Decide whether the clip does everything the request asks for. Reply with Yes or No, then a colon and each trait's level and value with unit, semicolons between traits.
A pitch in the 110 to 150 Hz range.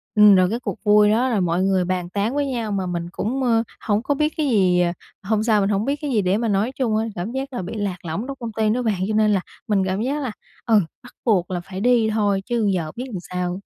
No: high, 210 Hz